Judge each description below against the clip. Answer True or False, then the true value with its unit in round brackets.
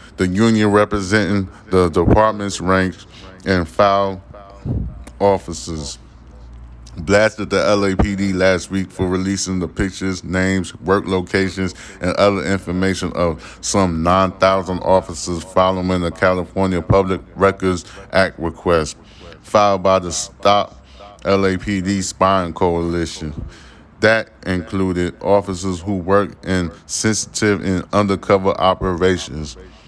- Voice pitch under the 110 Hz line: True (95 Hz)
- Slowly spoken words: True (105 wpm)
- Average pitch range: False (2.1 semitones)